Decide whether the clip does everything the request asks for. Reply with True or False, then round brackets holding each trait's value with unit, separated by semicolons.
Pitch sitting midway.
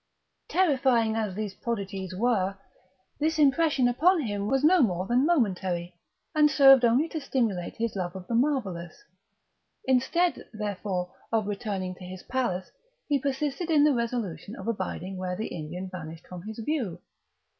False (225 Hz)